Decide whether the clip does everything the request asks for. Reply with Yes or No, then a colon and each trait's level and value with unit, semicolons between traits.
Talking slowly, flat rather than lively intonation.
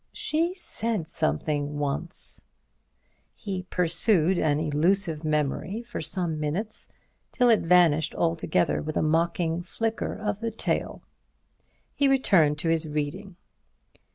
No: slow, 120 wpm; average, 5.1 semitones